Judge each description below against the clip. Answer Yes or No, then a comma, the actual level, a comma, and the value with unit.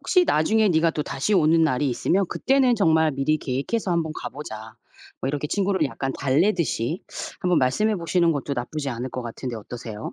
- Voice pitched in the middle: Yes, medium, 155 Hz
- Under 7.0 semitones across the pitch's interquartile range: Yes, wide, 5.5 semitones